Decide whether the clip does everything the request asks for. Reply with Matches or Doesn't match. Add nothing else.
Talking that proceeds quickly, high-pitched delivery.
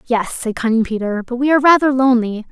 Matches